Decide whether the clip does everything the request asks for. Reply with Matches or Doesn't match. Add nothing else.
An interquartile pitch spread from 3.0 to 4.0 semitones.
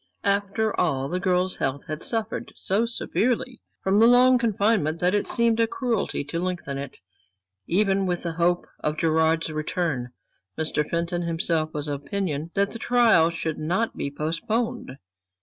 Doesn't match